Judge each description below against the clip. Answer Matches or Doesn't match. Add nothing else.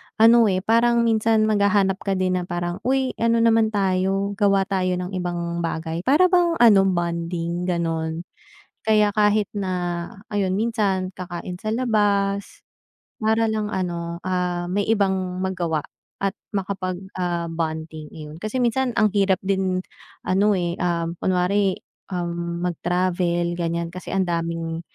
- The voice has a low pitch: Doesn't match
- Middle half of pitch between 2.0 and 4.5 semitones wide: Matches